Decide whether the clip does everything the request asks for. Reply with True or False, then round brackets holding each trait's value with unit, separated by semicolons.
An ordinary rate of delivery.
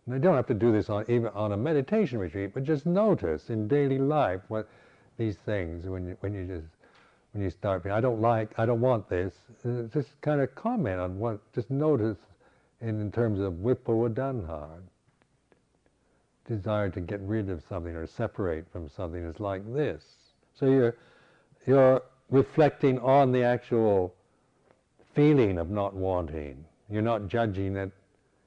True (170 wpm)